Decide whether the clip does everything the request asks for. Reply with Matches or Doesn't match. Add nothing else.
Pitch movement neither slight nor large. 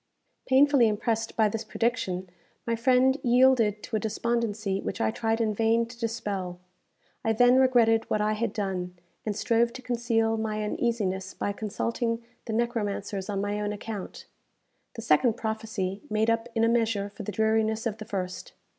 Doesn't match